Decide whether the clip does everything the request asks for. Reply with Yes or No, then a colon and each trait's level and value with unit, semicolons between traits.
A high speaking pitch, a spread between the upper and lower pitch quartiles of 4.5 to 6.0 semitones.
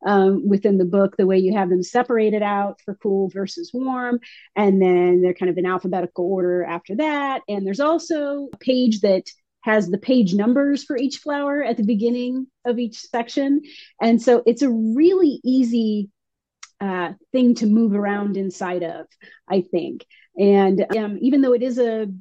Yes: high, 215 Hz; average, 4.8 semitones